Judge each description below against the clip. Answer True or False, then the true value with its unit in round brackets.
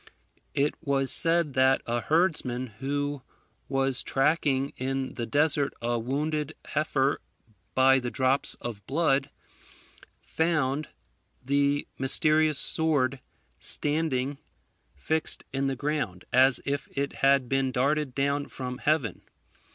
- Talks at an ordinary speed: False (115 wpm)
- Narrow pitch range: True (2.3 semitones)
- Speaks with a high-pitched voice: False (140 Hz)